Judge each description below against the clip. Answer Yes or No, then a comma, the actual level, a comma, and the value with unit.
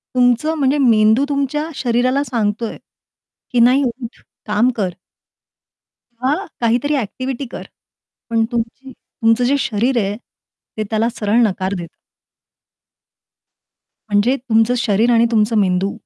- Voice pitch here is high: Yes, high, 235 Hz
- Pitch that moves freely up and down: No, average, 3.2 semitones